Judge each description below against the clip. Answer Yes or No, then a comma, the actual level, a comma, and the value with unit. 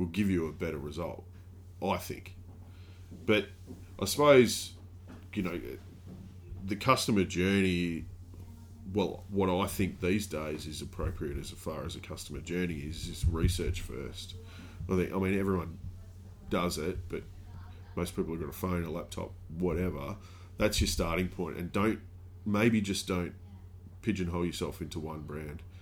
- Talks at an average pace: Yes, average, 150 wpm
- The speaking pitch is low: Yes, very low, 90 Hz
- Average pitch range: No, narrow, 1.5 semitones